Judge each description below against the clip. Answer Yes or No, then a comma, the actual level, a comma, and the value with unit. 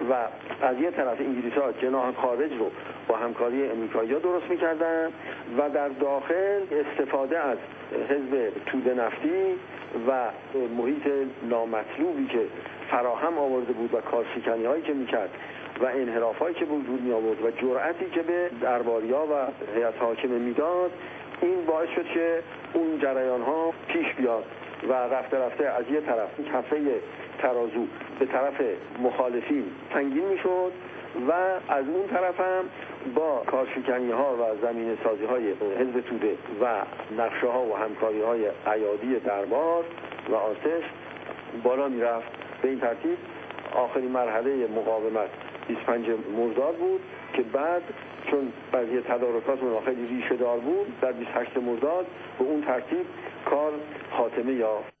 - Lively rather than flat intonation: Yes, wide, 5.8 semitones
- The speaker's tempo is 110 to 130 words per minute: No, average, 140 wpm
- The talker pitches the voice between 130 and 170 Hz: Yes, low, 135 Hz